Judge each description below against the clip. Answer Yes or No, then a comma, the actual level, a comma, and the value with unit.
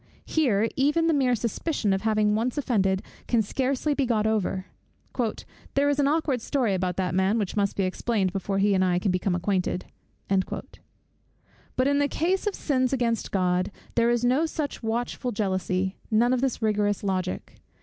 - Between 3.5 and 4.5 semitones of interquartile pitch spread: No, wide, 5.4 semitones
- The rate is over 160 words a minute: Yes, average, 175 wpm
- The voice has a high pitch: Yes, high, 220 Hz